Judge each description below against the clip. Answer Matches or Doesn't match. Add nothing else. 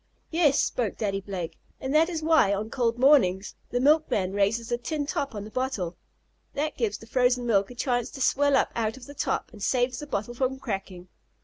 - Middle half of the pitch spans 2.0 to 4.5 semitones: Doesn't match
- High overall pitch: Matches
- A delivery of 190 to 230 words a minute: Matches